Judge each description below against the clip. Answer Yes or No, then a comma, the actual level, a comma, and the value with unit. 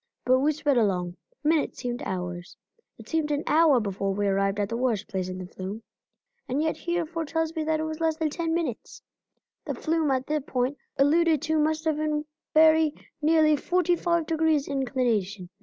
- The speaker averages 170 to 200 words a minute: Yes, average, 190 wpm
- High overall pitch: Yes, very high, 295 Hz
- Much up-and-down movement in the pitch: Yes, wide, 6.4 semitones